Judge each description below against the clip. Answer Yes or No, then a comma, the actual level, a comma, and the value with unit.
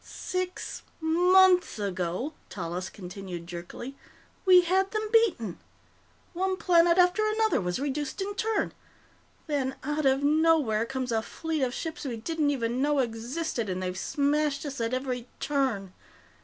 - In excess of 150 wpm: No, average, 140 wpm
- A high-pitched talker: Yes, very high, 280 Hz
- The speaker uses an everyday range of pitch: No, wide, 7.0 semitones